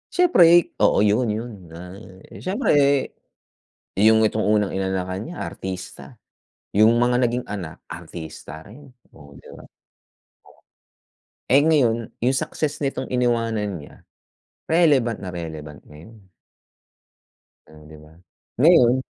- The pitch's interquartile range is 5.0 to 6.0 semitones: Yes, wide, 5.6 semitones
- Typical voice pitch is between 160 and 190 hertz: No, low, 110 Hz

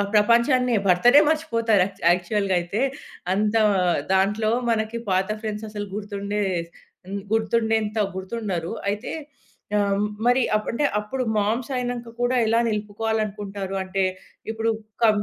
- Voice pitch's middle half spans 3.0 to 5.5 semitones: No, narrow, 2.4 semitones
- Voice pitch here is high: Yes, high, 215 Hz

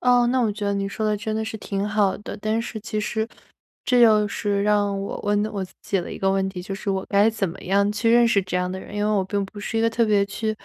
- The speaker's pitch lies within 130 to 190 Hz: No, high, 205 Hz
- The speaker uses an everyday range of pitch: No, narrow, 1.8 semitones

